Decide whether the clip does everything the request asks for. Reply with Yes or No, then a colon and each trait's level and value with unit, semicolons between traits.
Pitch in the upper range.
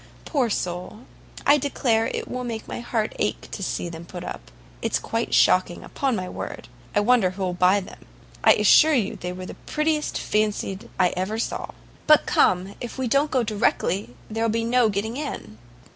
Yes: high, 215 Hz